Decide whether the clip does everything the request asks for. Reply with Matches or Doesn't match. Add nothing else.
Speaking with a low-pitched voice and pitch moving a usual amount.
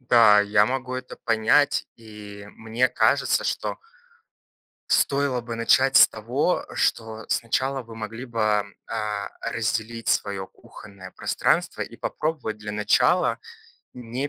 Matches